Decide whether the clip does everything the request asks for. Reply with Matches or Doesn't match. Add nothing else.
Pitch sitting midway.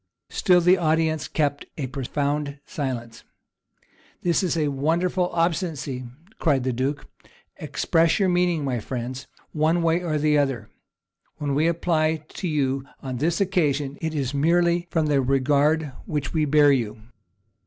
Matches